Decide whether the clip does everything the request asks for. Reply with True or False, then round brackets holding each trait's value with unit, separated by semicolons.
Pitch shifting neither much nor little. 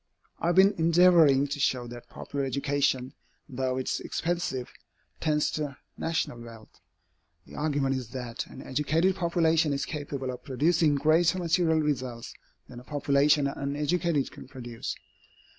True (3.7 semitones)